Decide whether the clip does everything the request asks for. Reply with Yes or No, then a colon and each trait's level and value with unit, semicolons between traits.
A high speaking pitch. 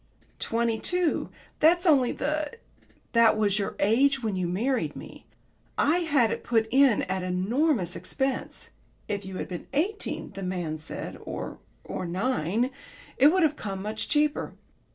Yes: high, 230 Hz